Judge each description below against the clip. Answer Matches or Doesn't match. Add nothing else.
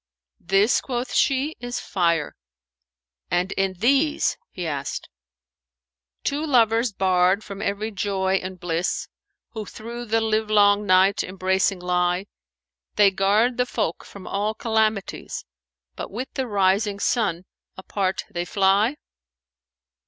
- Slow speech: Matches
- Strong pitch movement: Doesn't match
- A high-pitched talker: Matches